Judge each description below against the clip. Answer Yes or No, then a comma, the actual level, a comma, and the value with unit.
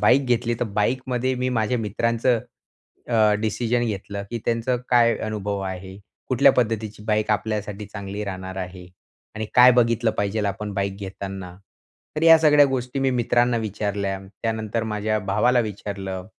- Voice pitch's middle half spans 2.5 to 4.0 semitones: Yes, average, 3.2 semitones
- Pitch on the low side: Yes, low, 110 Hz